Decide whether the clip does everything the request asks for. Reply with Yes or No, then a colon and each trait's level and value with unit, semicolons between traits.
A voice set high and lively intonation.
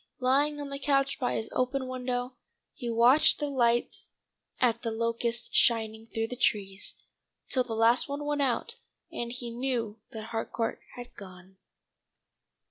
No: high, 240 Hz; average, 2.8 semitones